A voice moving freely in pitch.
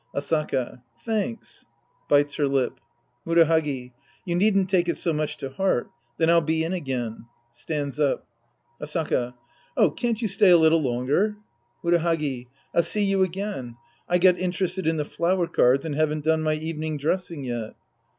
No: average, 4.1 semitones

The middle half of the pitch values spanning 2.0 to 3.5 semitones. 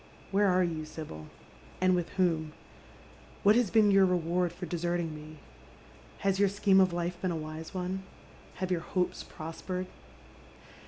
Yes: narrow, 2.6 semitones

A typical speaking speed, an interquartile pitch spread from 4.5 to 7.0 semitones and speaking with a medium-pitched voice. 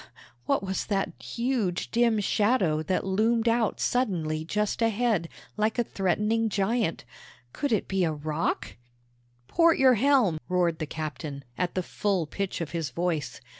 No: average, 155 wpm; wide, 5.5 semitones; high, 195 Hz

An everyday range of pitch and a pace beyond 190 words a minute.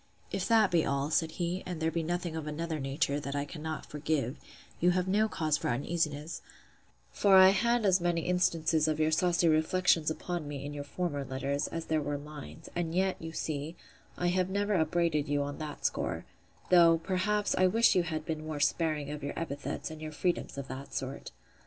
Yes: average, 3.2 semitones; average, 200 wpm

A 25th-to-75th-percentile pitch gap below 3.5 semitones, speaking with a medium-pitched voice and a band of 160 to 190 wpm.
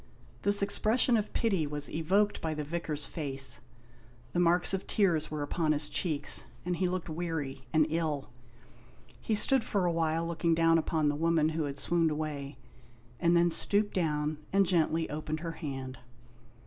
Yes: average, 2.8 semitones; medium, 165 Hz; average, 170 wpm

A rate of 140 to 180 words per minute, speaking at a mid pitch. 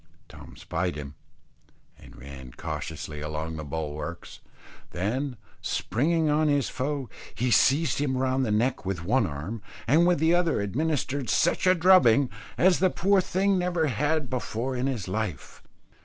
No: average, 155 wpm; low, 130 Hz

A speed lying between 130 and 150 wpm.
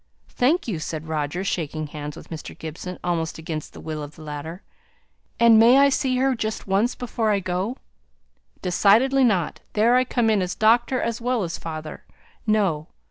No: average, 180 wpm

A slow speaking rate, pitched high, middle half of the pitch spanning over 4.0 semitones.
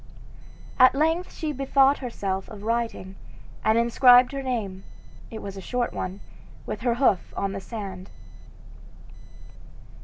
Yes: slow, 130 wpm; high, 235 Hz; average, 4.9 semitones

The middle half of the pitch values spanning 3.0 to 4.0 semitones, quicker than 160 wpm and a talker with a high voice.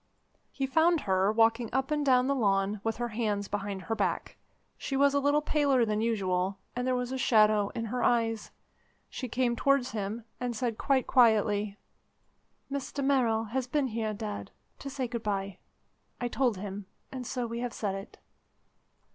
Yes: average, 3.7 semitones; average, 180 wpm; high, 230 Hz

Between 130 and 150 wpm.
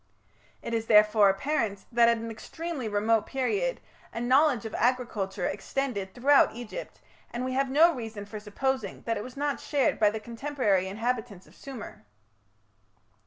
No: average, 160 wpm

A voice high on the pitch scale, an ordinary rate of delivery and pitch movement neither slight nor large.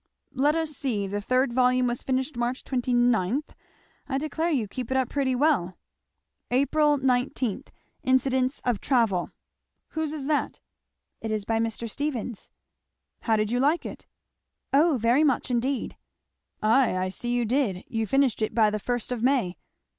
Yes: very high, 250 Hz; average, 160 wpm; average, 3.4 semitones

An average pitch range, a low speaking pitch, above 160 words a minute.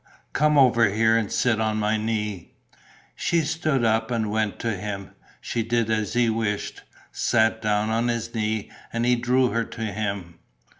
No: narrow, 1.8 semitones; low, 110 Hz; average, 170 wpm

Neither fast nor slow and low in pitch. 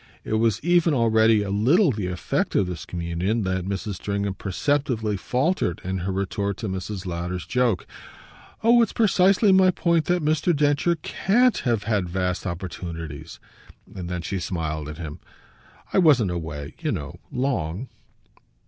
Yes: average, 155 wpm; low, 100 Hz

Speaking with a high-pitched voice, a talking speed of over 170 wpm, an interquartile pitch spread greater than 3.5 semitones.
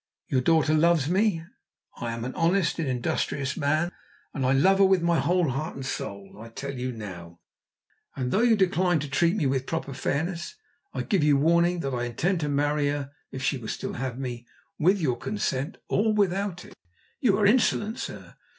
No: medium, 150 Hz; average, 200 wpm; average, 5.3 semitones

